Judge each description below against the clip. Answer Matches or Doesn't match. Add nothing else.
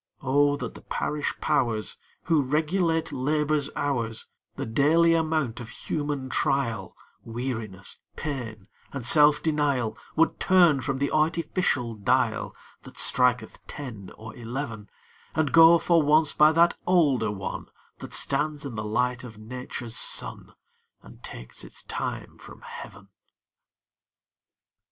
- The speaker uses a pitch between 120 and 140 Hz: Matches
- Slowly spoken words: Matches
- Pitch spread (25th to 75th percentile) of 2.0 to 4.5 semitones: Doesn't match